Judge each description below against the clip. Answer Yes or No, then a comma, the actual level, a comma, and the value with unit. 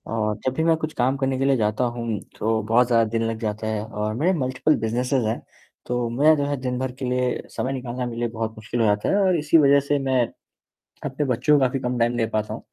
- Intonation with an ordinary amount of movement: Yes, average, 3.2 semitones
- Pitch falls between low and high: No, low, 125 Hz